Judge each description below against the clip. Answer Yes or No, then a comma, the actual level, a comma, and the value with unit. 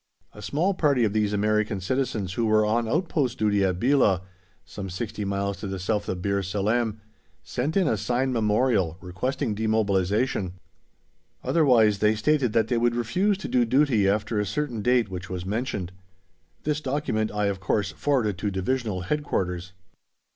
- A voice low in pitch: Yes, low, 110 Hz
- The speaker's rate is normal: Yes, average, 165 wpm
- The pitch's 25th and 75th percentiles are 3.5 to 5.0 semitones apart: Yes, average, 4.3 semitones